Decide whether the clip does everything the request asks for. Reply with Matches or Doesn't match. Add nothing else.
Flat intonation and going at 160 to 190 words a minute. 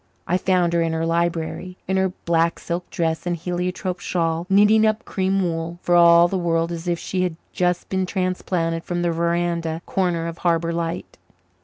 Matches